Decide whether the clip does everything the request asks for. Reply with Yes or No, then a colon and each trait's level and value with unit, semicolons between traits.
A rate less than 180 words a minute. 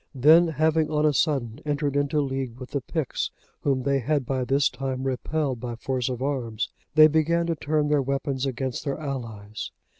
No: average, 185 wpm